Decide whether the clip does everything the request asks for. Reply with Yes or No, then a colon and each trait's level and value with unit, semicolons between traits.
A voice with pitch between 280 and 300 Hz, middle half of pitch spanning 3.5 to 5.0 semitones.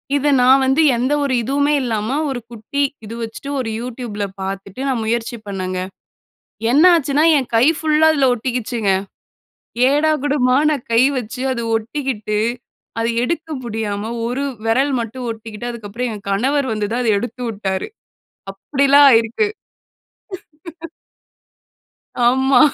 No: high, 245 Hz; average, 3.8 semitones